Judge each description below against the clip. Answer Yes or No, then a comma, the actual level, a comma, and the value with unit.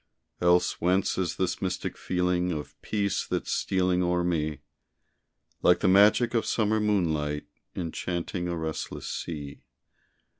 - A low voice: Yes, very low, 90 Hz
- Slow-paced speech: Yes, slow, 125 wpm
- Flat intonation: Yes, narrow, 2.1 semitones